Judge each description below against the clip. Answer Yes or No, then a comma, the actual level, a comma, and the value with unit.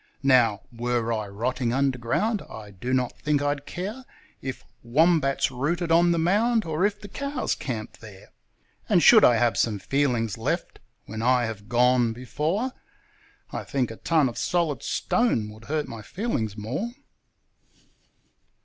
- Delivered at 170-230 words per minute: No, average, 150 wpm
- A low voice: Yes, low, 130 Hz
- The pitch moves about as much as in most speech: No, wide, 6.4 semitones